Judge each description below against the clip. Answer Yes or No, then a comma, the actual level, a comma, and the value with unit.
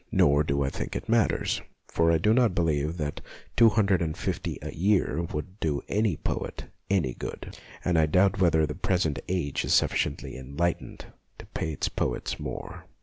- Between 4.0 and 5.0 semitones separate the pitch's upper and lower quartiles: Yes, average, 4.6 semitones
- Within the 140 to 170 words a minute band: No, average, 185 wpm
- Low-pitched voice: Yes, very low, 85 Hz